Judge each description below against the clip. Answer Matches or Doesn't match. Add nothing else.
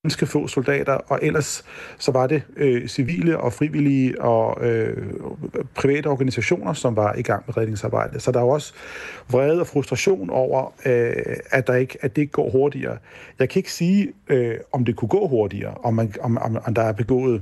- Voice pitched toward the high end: Doesn't match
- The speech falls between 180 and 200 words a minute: Matches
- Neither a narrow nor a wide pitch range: Matches